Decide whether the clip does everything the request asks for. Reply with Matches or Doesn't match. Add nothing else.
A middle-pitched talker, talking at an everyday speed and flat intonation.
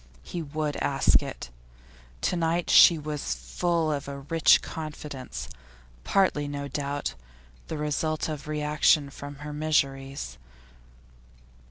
Doesn't match